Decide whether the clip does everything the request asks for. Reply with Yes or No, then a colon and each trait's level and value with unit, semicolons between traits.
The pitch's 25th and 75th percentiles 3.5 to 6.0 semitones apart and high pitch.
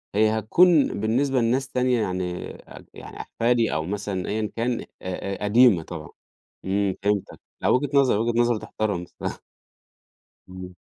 No: average, 4.1 semitones; low, 110 Hz